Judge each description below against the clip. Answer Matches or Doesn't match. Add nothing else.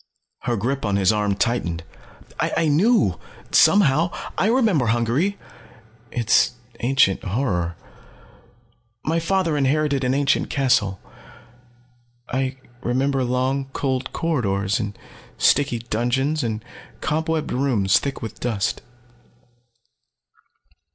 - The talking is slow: Matches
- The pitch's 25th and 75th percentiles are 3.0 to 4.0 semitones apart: Doesn't match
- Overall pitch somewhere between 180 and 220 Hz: Doesn't match